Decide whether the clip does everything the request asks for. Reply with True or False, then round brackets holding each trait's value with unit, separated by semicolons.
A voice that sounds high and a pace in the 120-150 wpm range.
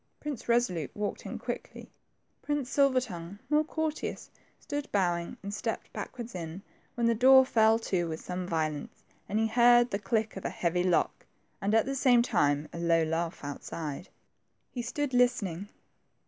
False (210 Hz; 165 wpm)